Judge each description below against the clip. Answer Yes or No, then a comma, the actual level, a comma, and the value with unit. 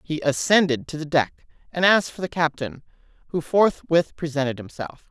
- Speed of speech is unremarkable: Yes, average, 165 wpm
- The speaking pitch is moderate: Yes, medium, 155 Hz